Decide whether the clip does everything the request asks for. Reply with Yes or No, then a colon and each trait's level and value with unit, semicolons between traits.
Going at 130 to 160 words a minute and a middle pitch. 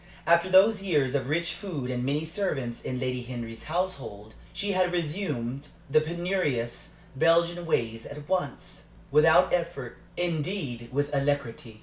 Yes: slow, 135 wpm; medium, 150 Hz